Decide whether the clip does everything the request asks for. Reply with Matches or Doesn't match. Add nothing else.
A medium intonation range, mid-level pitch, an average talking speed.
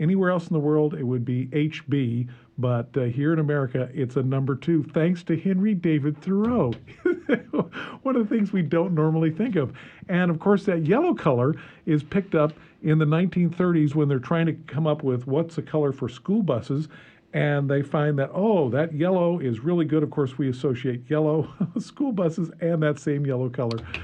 Matches